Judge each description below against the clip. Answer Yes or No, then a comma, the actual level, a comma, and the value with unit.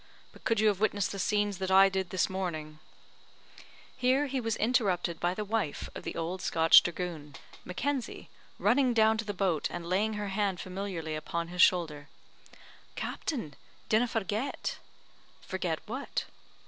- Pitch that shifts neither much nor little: Yes, average, 4.0 semitones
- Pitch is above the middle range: Yes, high, 195 Hz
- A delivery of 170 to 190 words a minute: No, average, 160 wpm